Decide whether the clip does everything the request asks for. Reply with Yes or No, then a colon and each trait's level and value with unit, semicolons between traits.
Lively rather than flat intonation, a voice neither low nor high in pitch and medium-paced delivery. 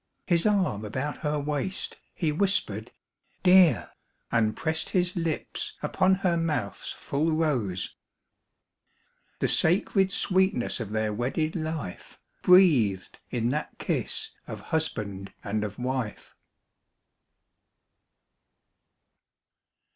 No: wide, 8.1 semitones; medium, 150 Hz; slow, 100 wpm